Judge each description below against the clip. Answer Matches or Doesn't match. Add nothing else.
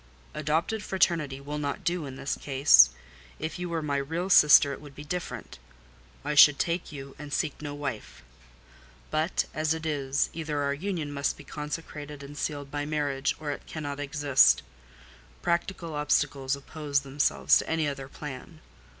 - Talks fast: Doesn't match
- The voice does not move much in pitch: Matches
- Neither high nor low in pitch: Matches